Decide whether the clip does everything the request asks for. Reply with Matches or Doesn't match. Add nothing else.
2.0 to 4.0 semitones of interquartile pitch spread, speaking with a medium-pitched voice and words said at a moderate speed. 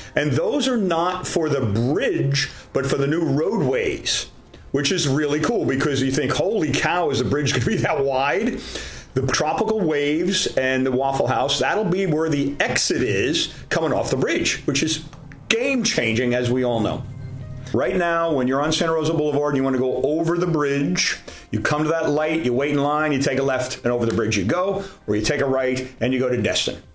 Doesn't match